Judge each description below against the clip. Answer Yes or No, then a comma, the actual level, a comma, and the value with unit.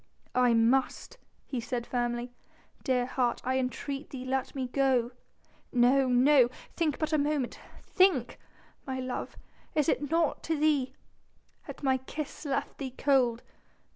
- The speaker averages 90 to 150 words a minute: Yes, average, 140 wpm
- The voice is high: Yes, very high, 260 Hz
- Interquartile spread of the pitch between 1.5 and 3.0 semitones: Yes, average, 2.7 semitones